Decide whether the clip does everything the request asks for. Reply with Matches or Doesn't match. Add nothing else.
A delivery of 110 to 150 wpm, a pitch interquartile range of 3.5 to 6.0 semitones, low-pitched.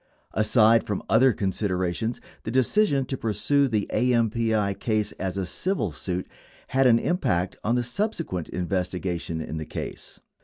Matches